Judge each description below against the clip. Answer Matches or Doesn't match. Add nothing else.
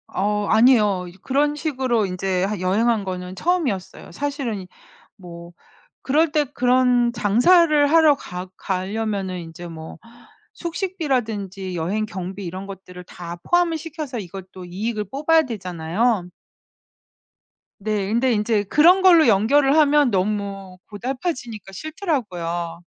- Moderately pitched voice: Doesn't match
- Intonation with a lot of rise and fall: Matches